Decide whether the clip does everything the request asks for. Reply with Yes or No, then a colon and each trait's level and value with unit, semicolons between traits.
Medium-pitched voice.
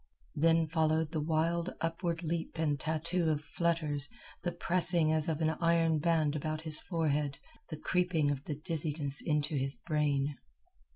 Yes: medium, 160 Hz